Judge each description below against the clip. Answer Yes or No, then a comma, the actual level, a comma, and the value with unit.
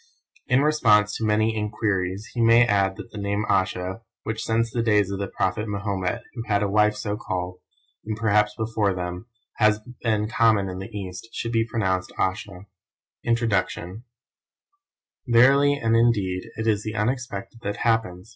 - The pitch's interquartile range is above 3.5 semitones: No, average, 2.7 semitones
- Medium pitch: No, low, 105 Hz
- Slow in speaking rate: No, average, 165 wpm